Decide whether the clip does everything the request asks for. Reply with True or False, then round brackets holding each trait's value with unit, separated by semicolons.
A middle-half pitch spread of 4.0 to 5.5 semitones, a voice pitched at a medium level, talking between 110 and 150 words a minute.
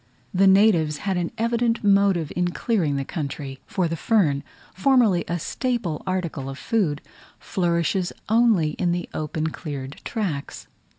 True (5.1 semitones; 175 Hz; 140 wpm)